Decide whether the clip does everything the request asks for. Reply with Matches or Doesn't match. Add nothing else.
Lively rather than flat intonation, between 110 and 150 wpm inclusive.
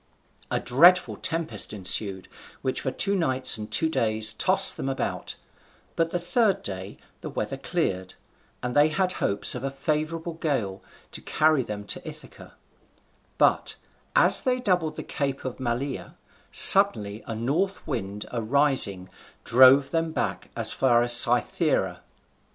Matches